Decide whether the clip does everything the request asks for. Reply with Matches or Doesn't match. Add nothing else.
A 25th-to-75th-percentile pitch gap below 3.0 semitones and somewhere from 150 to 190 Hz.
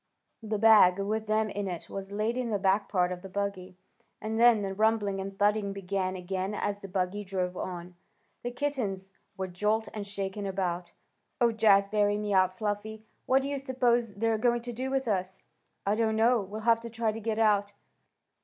Doesn't match